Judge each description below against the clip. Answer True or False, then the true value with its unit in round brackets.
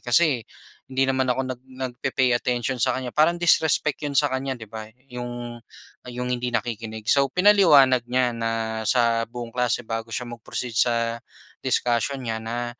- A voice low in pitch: True (120 Hz)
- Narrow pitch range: True (2.3 semitones)